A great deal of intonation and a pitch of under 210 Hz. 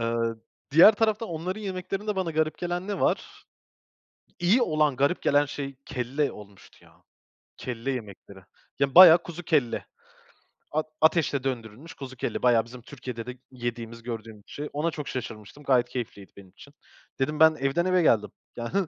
Yes: wide, 5.9 semitones; medium, 140 Hz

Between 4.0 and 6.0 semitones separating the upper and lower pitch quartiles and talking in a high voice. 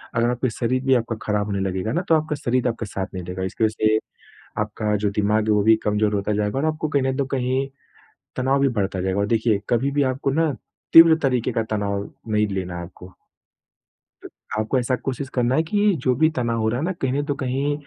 No: average, 4.5 semitones; low, 120 Hz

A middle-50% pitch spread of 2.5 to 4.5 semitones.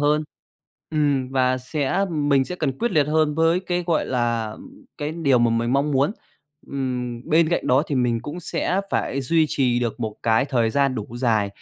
Yes: average, 4.1 semitones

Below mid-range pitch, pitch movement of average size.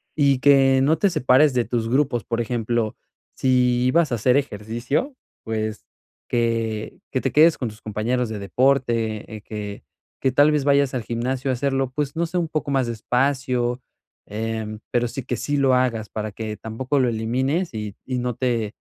Yes: low, 125 Hz; average, 3.4 semitones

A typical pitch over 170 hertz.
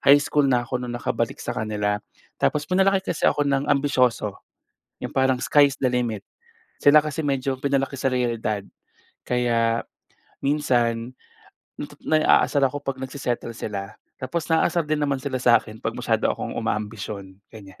No: low, 130 Hz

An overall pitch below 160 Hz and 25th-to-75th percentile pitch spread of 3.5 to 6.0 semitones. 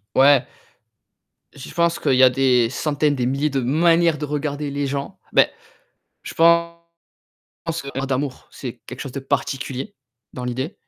No: medium, 140 Hz; narrow, 2.6 semitones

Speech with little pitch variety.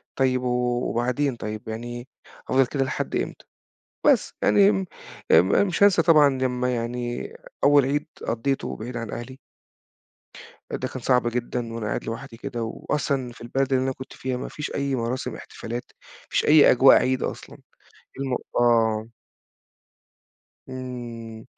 Yes: narrow, 2.3 semitones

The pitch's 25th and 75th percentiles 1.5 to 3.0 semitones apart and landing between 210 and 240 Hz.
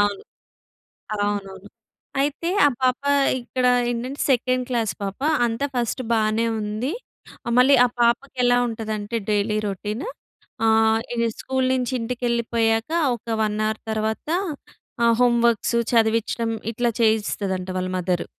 Yes: narrow, 2.4 semitones; high, 225 Hz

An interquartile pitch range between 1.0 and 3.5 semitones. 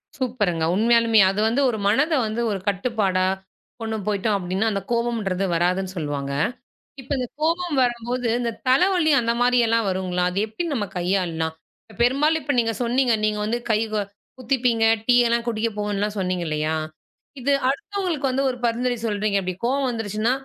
No: average, 4.1 semitones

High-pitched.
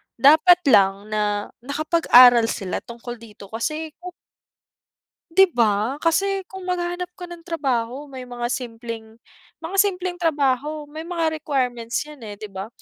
Yes: very high, 275 Hz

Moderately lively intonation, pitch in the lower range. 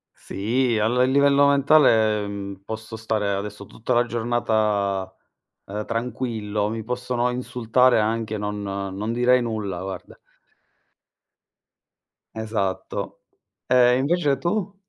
Yes: average, 3.2 semitones; low, 115 Hz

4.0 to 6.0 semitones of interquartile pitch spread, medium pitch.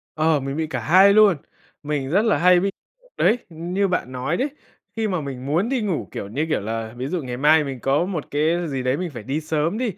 Yes: average, 5.1 semitones; medium, 155 Hz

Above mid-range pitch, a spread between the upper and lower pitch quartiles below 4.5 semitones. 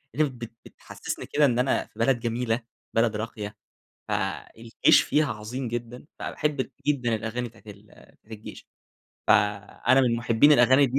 No: low, 120 Hz; average, 2.7 semitones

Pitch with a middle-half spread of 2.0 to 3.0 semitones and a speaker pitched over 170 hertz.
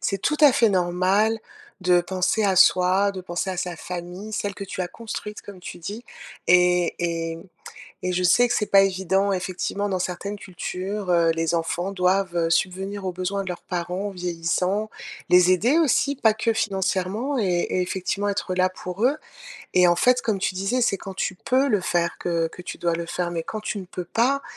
Yes: narrow, 2.4 semitones; medium, 185 Hz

